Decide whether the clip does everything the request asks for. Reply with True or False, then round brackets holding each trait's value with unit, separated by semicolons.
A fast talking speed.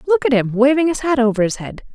True (275 wpm)